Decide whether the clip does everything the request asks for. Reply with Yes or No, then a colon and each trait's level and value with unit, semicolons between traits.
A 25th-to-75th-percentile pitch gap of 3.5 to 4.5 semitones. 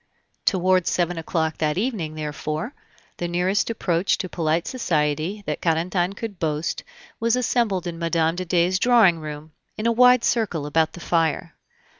Yes: average, 4.0 semitones